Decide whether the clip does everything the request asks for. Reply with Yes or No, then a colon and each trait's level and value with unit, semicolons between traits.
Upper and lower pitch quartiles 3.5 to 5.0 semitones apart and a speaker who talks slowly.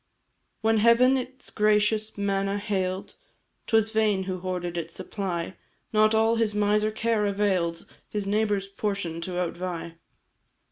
No: average, 2.8 semitones; slow, 130 wpm